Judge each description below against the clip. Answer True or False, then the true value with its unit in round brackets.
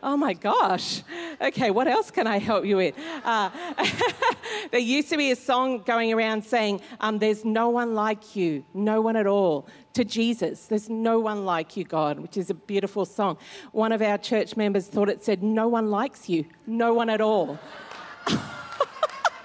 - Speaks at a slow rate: False (185 wpm)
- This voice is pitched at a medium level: False (220 Hz)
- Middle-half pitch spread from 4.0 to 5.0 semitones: False (3.2 semitones)